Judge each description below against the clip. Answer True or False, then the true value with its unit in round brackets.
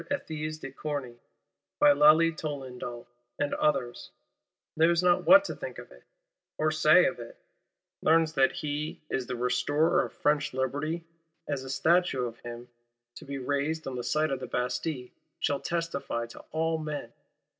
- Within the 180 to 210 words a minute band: False (155 wpm)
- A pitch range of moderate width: True (3.7 semitones)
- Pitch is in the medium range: True (145 Hz)